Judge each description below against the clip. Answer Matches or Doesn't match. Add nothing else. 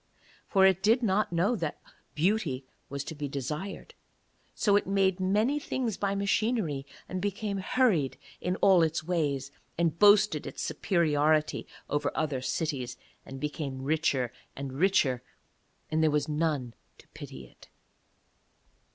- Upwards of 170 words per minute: Doesn't match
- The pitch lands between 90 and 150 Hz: Doesn't match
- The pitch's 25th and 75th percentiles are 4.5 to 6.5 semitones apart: Matches